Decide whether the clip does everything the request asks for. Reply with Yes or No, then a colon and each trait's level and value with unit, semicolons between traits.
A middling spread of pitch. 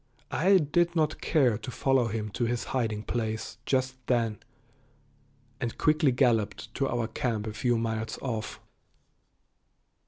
Yes: average, 3.2 semitones